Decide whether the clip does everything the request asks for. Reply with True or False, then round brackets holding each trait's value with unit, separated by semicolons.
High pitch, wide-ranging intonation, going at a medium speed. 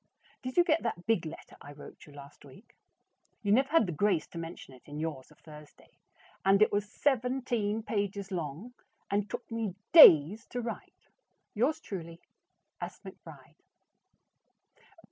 True (200 Hz; 6.6 semitones; 155 wpm)